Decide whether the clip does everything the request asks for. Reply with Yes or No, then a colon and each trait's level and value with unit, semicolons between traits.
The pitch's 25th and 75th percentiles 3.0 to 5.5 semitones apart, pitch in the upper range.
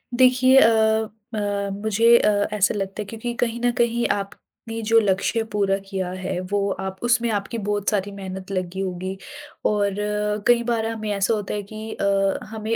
No: narrow, 2.5 semitones; high, 210 Hz